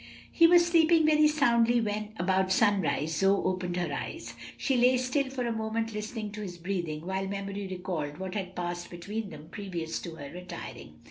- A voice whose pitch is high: Yes, high, 200 Hz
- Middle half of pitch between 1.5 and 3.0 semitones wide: No, average, 4.8 semitones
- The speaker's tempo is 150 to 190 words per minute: Yes, average, 185 wpm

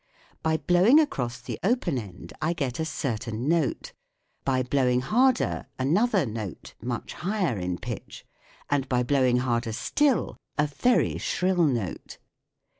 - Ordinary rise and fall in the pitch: No, wide, 6.6 semitones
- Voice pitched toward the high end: No, medium, 140 Hz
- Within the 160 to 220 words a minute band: No, average, 140 wpm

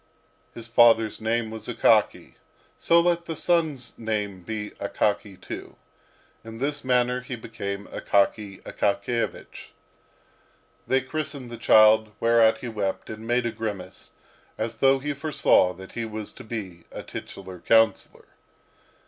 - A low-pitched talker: Yes, low, 115 Hz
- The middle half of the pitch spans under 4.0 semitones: Yes, average, 3.0 semitones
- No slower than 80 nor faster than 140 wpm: Yes, slow, 135 wpm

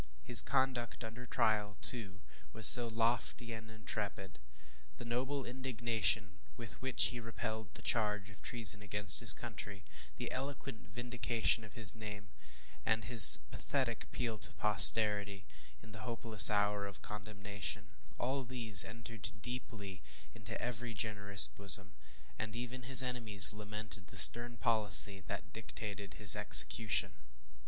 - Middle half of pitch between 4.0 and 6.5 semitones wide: No, narrow, 2.6 semitones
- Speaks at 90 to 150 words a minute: Yes, slow, 135 wpm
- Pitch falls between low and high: No, low, 110 Hz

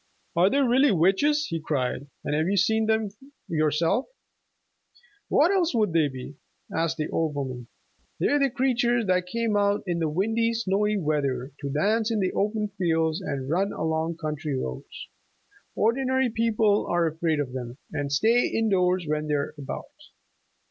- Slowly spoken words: No, average, 155 wpm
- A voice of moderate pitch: Yes, medium, 180 Hz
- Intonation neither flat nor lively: No, wide, 6.7 semitones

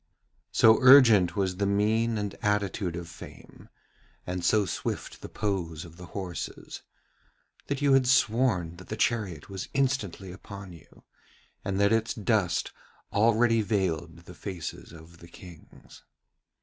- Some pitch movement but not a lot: Yes, average, 4.1 semitones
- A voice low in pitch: Yes, low, 100 Hz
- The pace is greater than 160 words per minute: No, average, 140 wpm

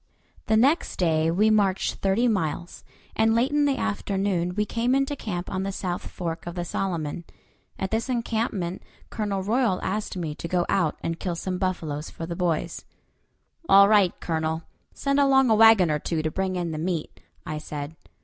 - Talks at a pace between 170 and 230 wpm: Yes, average, 185 wpm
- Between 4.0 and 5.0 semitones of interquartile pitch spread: Yes, average, 4.6 semitones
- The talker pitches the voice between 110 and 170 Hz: No, medium, 185 Hz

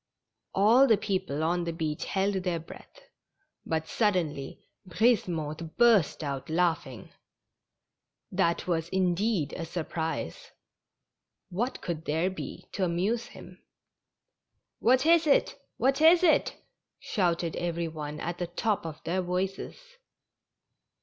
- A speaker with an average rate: No, slow, 125 wpm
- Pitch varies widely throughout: No, average, 4.1 semitones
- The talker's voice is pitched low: No, medium, 175 Hz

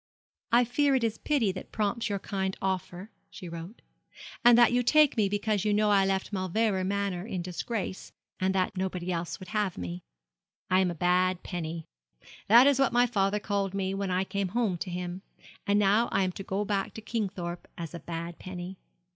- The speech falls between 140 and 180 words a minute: No, average, 200 wpm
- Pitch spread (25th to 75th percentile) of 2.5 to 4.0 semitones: Yes, average, 2.8 semitones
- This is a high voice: Yes, high, 195 Hz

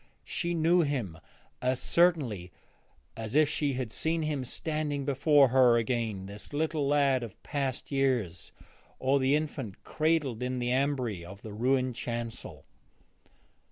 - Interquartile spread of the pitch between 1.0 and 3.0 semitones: No, average, 3.9 semitones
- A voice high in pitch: No, low, 130 Hz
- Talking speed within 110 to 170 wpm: Yes, average, 140 wpm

